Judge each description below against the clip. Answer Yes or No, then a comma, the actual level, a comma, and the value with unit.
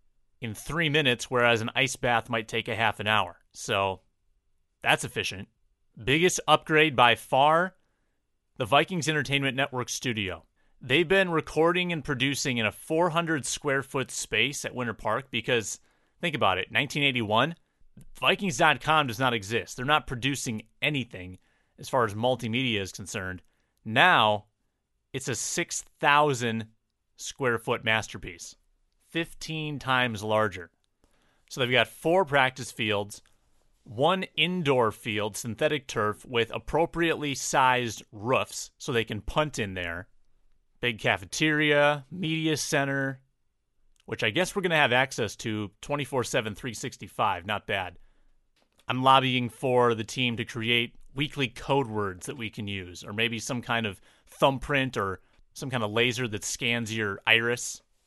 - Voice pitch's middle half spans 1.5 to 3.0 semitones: No, average, 4.8 semitones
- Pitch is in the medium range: No, low, 125 Hz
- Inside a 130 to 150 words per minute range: Yes, average, 140 wpm